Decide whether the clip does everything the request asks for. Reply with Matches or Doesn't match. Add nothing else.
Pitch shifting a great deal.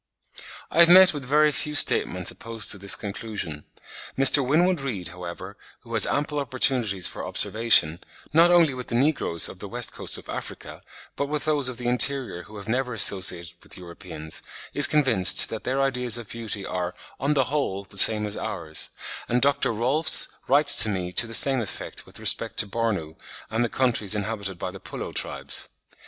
Matches